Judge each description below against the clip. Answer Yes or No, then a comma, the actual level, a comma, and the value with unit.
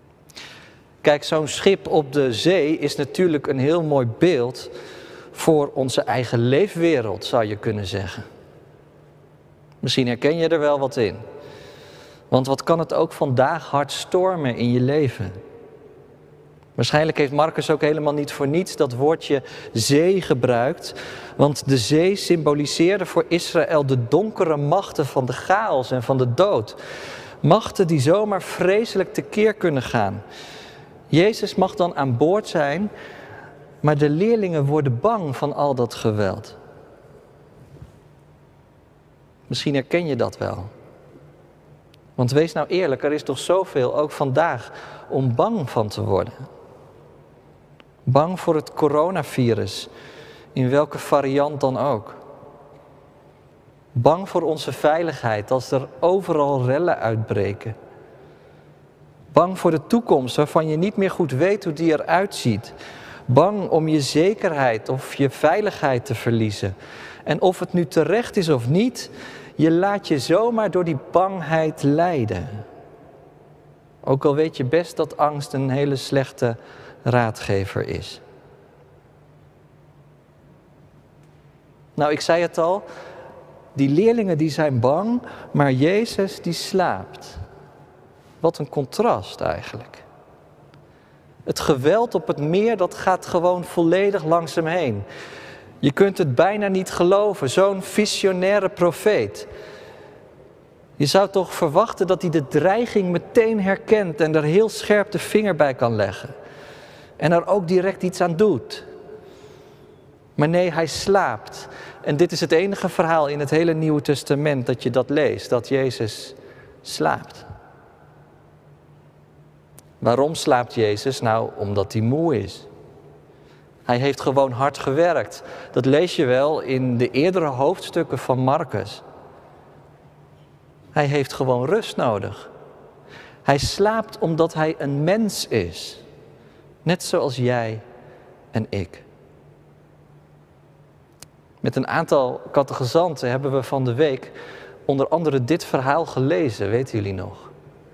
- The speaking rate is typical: No, slow, 130 wpm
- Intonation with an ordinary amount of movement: Yes, average, 4.7 semitones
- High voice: No, medium, 150 Hz